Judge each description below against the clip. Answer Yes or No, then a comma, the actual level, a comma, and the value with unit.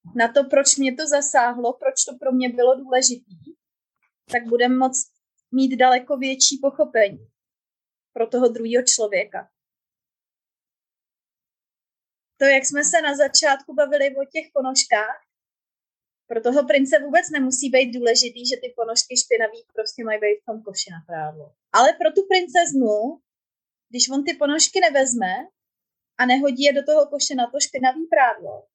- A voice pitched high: Yes, very high, 260 Hz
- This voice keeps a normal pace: Yes, average, 150 wpm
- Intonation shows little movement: No, average, 3.3 semitones